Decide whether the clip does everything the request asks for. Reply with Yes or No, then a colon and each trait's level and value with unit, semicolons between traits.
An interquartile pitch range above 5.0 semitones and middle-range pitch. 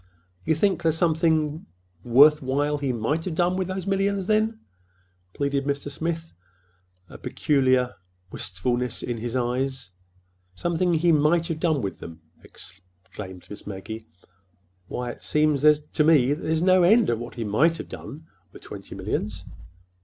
Yes: wide, 5.5 semitones; medium, 145 Hz